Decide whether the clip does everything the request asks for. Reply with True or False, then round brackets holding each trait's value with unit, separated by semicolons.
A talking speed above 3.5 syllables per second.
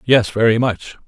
True (4.7 syllables/s)